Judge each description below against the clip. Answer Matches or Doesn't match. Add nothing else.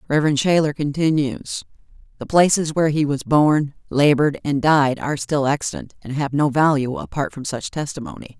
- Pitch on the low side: Doesn't match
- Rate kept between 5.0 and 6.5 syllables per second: Matches